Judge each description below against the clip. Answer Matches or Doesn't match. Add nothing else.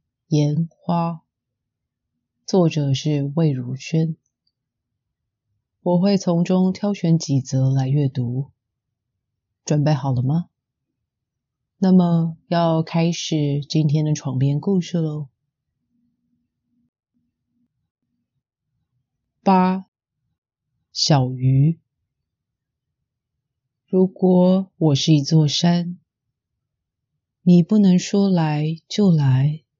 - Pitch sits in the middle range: Matches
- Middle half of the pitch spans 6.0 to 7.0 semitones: Doesn't match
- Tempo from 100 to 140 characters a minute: Matches